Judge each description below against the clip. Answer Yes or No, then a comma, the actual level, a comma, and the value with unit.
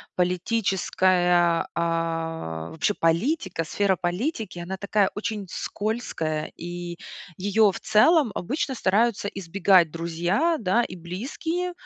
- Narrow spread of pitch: No, average, 4.3 semitones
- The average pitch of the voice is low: No, medium, 185 Hz